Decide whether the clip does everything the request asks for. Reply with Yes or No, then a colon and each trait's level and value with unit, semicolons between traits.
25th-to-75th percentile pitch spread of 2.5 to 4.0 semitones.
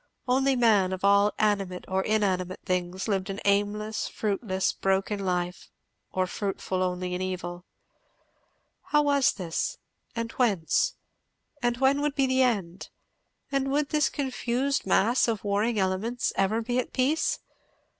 No: average, 5.0 semitones